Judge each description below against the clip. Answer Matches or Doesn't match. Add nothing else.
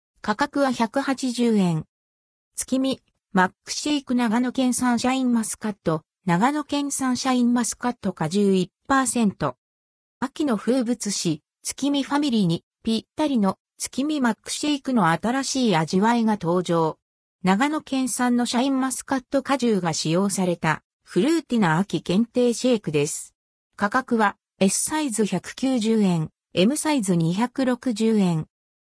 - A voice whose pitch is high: Matches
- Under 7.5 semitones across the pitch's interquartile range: Matches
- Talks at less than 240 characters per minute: Doesn't match